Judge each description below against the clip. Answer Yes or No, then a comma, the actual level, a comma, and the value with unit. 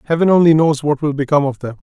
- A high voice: No, medium, 150 Hz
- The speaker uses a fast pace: Yes, fast, 260 wpm